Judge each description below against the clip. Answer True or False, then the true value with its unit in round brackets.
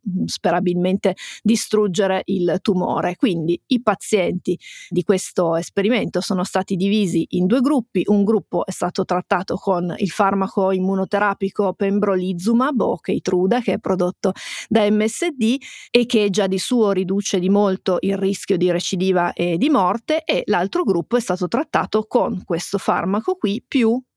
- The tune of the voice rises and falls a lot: False (2.7 semitones)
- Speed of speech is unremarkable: True (150 wpm)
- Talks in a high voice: True (195 Hz)